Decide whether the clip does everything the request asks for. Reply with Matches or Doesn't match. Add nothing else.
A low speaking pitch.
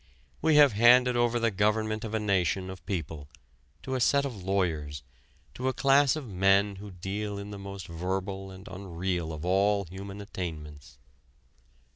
Matches